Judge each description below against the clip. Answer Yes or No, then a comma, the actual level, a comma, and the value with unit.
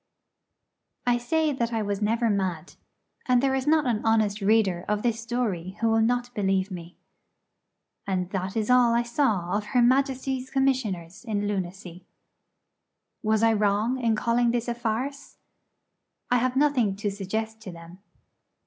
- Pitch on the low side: No, high, 225 Hz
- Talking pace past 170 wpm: No, average, 155 wpm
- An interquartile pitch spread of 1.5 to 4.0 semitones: Yes, average, 3.7 semitones